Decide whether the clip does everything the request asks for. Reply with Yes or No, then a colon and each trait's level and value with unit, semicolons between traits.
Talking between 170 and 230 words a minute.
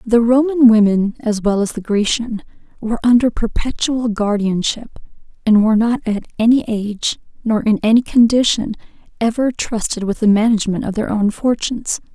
No: average, 155 wpm